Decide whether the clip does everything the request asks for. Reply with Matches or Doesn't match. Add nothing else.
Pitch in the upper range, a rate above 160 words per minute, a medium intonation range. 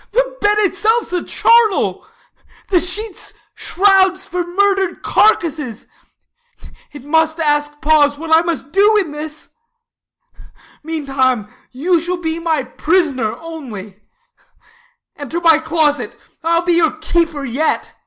Doesn't match